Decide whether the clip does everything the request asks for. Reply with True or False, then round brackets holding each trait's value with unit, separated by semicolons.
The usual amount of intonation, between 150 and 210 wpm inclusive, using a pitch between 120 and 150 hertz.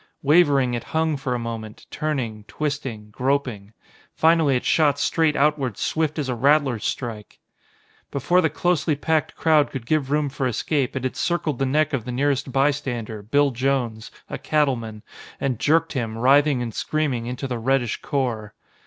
True (3.8 semitones; 165 wpm; 135 Hz)